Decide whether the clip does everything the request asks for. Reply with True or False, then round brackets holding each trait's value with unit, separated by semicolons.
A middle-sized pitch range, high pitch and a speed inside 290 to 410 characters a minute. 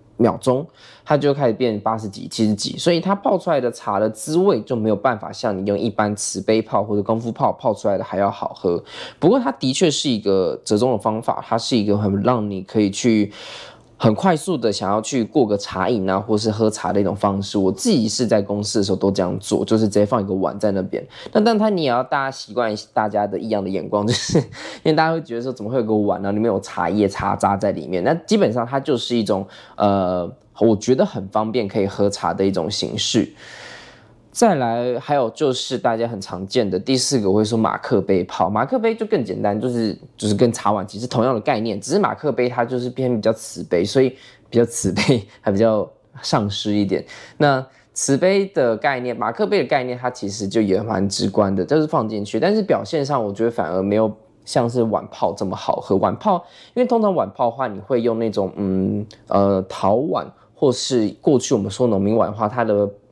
False (3.9 semitones; 110 Hz; 320 characters per minute)